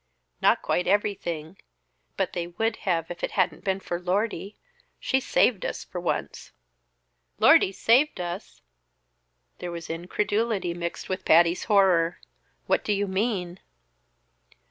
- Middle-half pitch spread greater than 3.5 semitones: No, average, 3.0 semitones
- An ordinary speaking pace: No, slow, 130 wpm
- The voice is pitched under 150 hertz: No, medium, 185 Hz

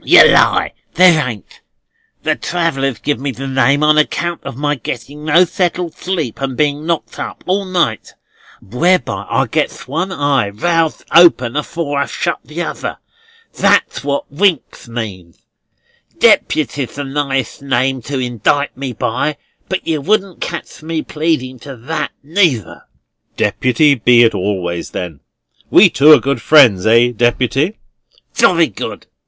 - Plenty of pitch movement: No, average, 4.9 semitones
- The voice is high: No, medium, 140 Hz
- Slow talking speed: No, average, 145 wpm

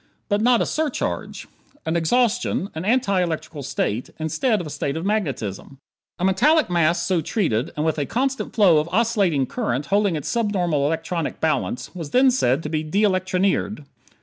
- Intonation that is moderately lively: No, wide, 5.7 semitones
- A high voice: No, medium, 175 Hz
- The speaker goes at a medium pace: Yes, average, 175 wpm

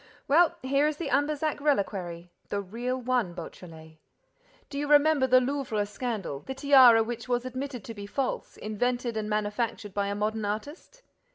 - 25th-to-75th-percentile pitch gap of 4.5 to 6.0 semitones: Yes, average, 5.1 semitones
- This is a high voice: Yes, high, 240 Hz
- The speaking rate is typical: Yes, average, 165 wpm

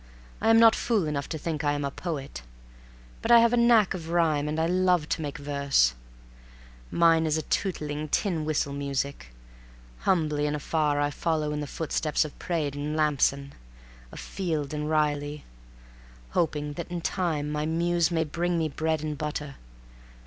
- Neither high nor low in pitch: Yes, medium, 155 Hz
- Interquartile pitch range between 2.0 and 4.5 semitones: Yes, narrow, 2.6 semitones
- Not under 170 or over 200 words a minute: Yes, average, 175 wpm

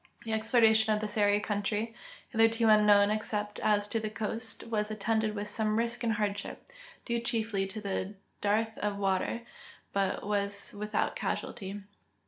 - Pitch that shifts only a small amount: Yes, narrow, 1.5 semitones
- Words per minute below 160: Yes, average, 150 wpm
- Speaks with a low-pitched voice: No, high, 210 Hz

